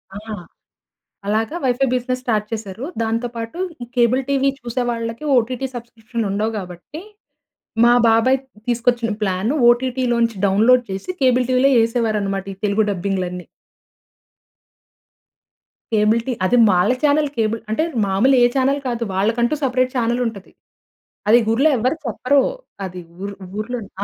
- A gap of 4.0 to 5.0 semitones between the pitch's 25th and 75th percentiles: No, average, 3.1 semitones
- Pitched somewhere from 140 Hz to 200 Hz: No, high, 230 Hz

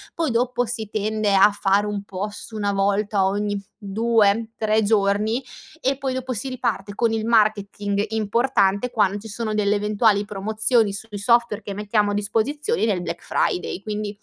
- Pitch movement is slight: Yes, narrow, 2.1 semitones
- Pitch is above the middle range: Yes, high, 210 Hz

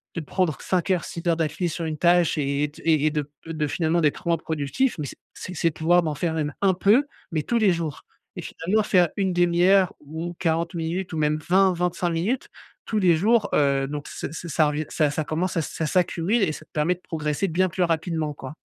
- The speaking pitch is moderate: Yes, medium, 165 Hz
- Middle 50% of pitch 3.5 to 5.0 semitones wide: No, average, 2.9 semitones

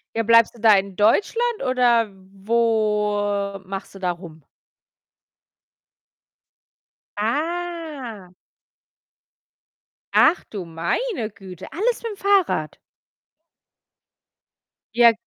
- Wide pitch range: Yes, wide, 7.9 semitones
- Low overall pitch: No, high, 225 Hz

